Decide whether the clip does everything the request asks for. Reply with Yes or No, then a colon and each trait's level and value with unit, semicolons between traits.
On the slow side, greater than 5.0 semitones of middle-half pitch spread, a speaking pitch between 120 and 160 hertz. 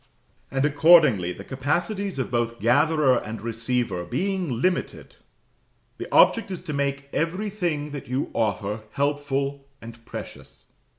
Yes: slow, 125 wpm; wide, 5.5 semitones; medium, 140 Hz